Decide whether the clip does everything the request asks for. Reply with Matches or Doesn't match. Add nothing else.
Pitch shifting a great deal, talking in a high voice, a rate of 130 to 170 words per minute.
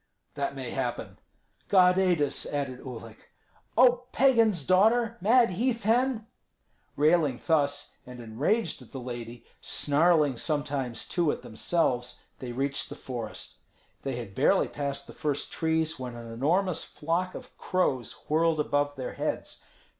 Doesn't match